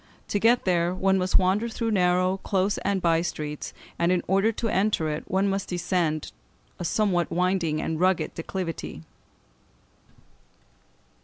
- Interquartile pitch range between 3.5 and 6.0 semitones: No, narrow, 2.4 semitones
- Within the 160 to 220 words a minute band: No, average, 145 wpm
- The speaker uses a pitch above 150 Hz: Yes, medium, 185 Hz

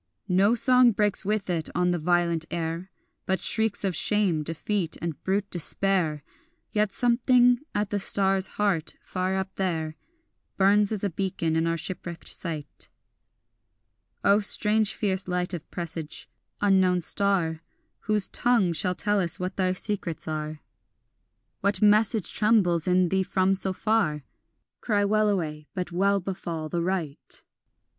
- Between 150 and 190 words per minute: No, average, 140 wpm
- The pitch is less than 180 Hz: No, high, 190 Hz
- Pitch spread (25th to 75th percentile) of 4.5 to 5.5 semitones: No, average, 3.3 semitones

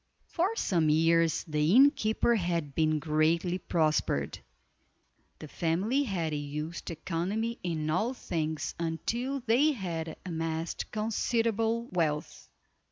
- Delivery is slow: Yes, slow, 105 wpm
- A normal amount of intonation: No, wide, 6.1 semitones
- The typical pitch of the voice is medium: Yes, medium, 170 Hz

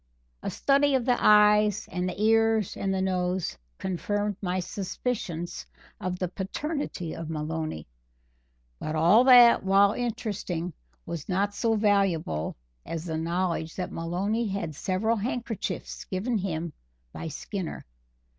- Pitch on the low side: No, high, 190 Hz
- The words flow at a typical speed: No, slow, 130 wpm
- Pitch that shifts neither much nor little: Yes, average, 4.0 semitones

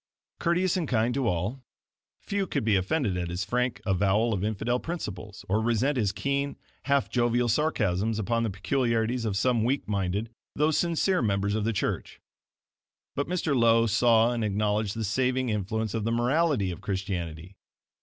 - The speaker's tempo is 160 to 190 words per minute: Yes, average, 165 wpm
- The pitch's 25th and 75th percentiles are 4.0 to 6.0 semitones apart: Yes, average, 4.3 semitones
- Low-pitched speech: Yes, low, 115 Hz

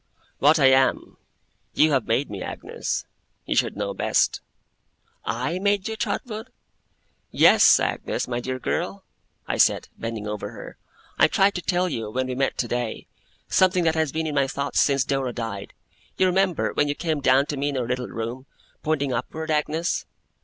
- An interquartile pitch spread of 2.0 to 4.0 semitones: No, average, 4.7 semitones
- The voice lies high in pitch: No, medium, 140 Hz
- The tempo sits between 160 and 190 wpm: Yes, average, 175 wpm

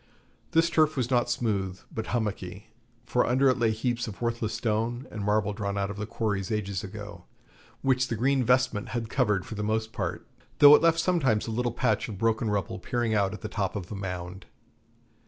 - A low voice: Yes, low, 110 Hz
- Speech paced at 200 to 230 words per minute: Yes, fast, 205 wpm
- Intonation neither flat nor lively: Yes, average, 3.0 semitones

